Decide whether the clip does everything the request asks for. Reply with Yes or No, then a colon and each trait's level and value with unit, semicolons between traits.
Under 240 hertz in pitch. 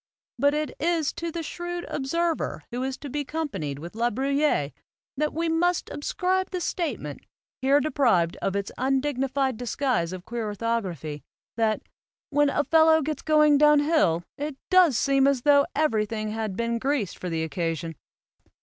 No: very high, 270 Hz